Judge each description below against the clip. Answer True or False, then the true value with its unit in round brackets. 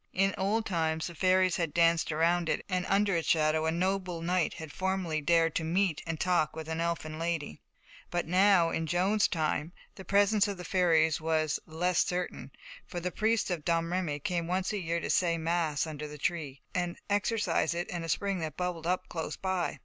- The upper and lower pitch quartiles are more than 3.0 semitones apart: False (2.5 semitones)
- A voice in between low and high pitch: True (170 Hz)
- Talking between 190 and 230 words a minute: True (200 wpm)